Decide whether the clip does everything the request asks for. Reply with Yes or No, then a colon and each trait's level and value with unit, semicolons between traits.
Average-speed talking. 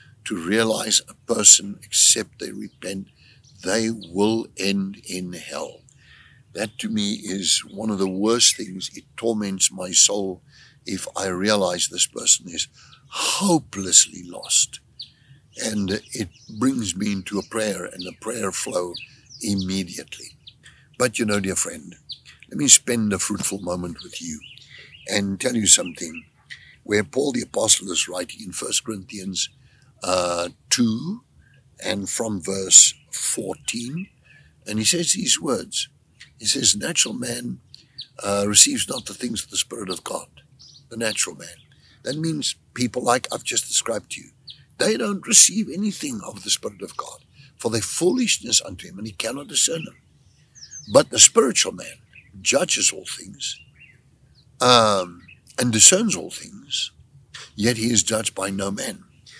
Yes: average, 145 wpm